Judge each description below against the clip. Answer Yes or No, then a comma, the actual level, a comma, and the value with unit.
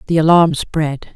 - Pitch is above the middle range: No, medium, 160 Hz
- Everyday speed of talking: Yes, average, 155 wpm